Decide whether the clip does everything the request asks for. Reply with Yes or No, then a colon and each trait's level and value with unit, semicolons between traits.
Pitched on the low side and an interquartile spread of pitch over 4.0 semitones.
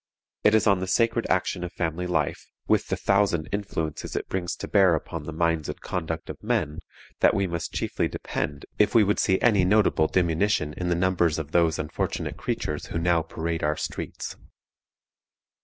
No: very low, 85 Hz; average, 3.3 semitones